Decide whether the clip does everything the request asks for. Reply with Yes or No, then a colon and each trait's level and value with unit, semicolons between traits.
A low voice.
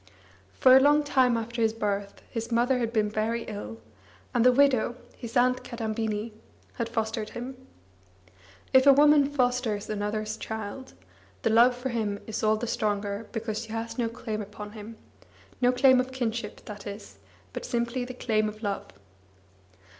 No: high, 230 Hz